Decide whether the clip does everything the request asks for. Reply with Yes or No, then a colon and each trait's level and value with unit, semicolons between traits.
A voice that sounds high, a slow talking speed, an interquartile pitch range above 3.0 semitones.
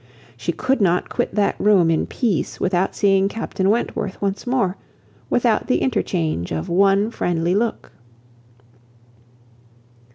Yes: high, 195 Hz; slow, 125 wpm; average, 3.7 semitones